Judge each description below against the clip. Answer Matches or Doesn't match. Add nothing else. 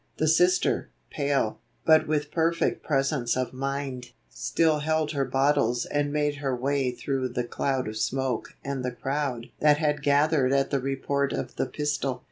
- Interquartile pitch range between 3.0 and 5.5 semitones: Doesn't match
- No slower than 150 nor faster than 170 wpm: Matches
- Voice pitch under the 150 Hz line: Matches